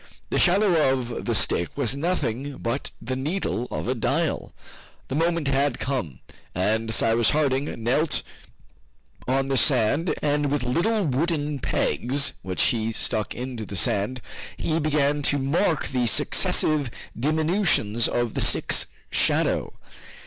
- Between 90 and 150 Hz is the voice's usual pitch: Yes, low, 135 Hz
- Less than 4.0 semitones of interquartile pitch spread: No, average, 4.4 semitones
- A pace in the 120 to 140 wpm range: Yes, slow, 135 wpm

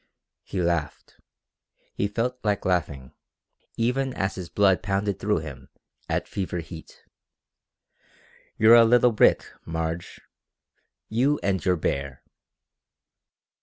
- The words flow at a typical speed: No, slow, 110 wpm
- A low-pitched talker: Yes, very low, 95 Hz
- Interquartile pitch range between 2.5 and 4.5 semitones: No, wide, 5.4 semitones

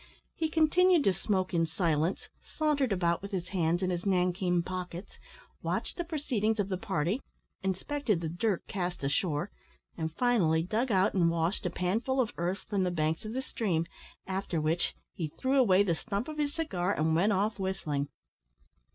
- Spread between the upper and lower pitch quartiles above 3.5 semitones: Yes, average, 4.6 semitones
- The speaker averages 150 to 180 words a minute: Yes, average, 175 wpm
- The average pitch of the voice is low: No, high, 190 Hz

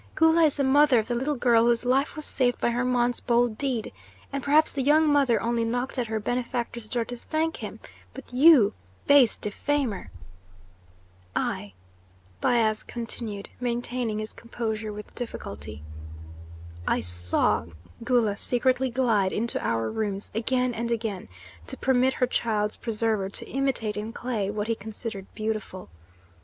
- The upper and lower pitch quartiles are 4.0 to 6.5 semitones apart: No, average, 3.1 semitones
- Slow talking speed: No, average, 150 wpm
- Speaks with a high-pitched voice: Yes, high, 235 Hz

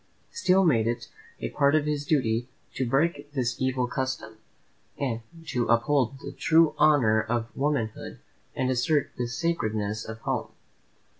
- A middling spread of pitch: Yes, average, 4.1 semitones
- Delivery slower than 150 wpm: Yes, average, 140 wpm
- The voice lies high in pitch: No, low, 130 Hz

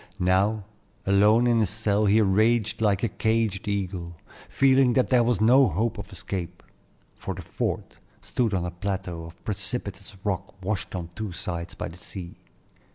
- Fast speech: No, average, 165 wpm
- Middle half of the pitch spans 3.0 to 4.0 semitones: Yes, average, 3.3 semitones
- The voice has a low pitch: Yes, low, 100 Hz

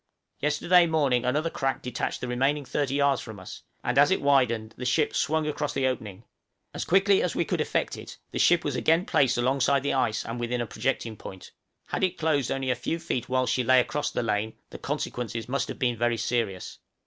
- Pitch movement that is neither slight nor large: Yes, average, 3.6 semitones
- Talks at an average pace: No, fast, 215 wpm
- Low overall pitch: Yes, low, 130 Hz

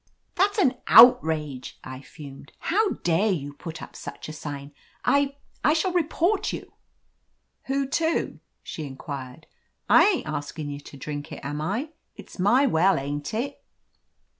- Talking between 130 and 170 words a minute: Yes, average, 160 wpm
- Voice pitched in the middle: Yes, medium, 165 Hz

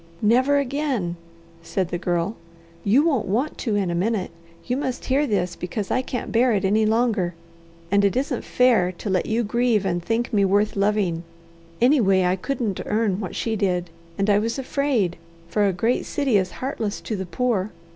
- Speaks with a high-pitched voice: Yes, high, 215 Hz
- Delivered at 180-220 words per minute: Yes, average, 185 wpm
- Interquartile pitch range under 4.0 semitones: No, average, 4.7 semitones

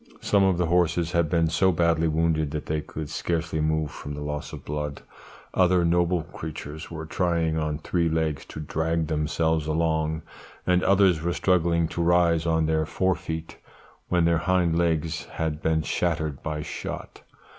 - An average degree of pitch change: No, narrow, 1.7 semitones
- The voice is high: No, very low, 80 Hz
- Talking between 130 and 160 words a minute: No, average, 170 wpm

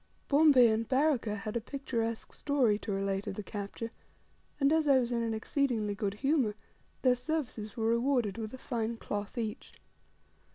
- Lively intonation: No, average, 4.1 semitones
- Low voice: No, high, 230 Hz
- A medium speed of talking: Yes, average, 170 wpm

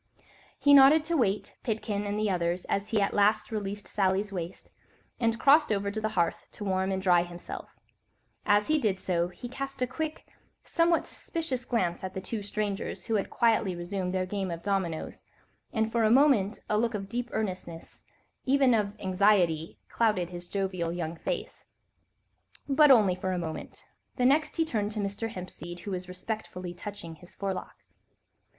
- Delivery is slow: No, average, 180 wpm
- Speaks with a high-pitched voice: Yes, high, 205 Hz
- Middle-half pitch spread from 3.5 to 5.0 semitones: Yes, average, 3.9 semitones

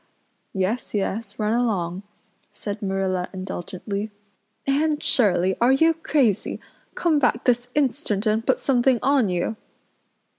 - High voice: Yes, high, 220 Hz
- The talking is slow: Yes, slow, 120 wpm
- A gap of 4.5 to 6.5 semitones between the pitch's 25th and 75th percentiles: Yes, wide, 5.5 semitones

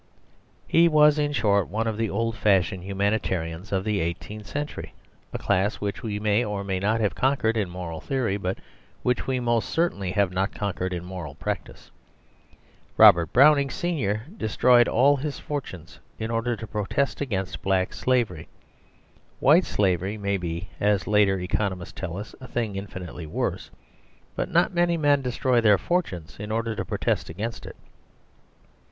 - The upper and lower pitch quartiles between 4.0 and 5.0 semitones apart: Yes, average, 4.5 semitones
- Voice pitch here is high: No, low, 105 Hz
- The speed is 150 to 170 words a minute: Yes, average, 160 wpm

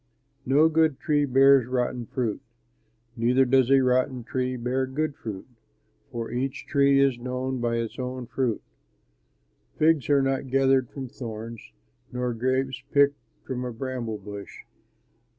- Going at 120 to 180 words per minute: Yes, average, 140 wpm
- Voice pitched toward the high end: No, low, 130 Hz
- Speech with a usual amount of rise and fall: No, narrow, 2.0 semitones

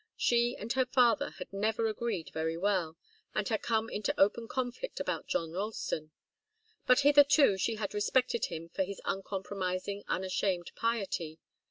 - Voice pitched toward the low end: No, high, 205 Hz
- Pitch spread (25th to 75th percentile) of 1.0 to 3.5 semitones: No, average, 4.2 semitones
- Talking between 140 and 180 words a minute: Yes, average, 150 wpm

